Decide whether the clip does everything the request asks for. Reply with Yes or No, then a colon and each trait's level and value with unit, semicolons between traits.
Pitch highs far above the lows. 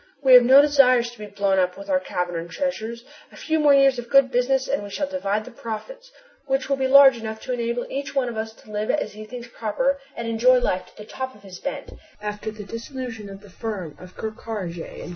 No: average, 4.3 semitones